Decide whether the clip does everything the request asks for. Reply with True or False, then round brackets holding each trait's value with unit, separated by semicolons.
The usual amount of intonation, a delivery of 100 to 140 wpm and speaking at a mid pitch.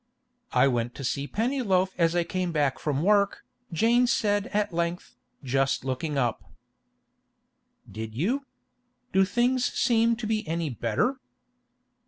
False (8.2 semitones; 135 wpm; 175 Hz)